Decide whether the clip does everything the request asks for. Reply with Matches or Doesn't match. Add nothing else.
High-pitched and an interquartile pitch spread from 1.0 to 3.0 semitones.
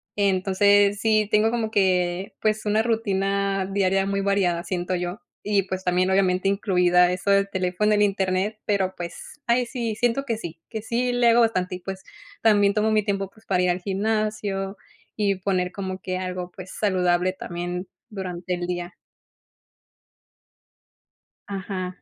Matches